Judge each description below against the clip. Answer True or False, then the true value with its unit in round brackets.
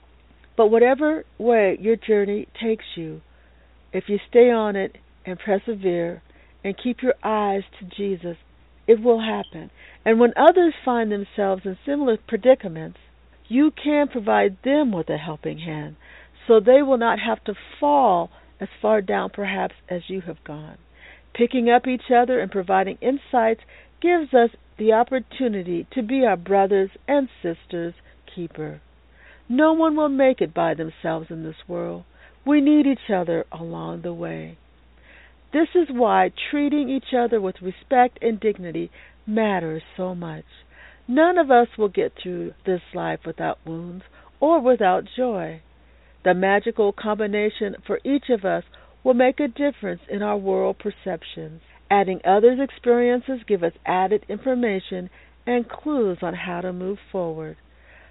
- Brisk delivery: False (150 wpm)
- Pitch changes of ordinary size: False (6.0 semitones)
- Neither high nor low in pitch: False (205 Hz)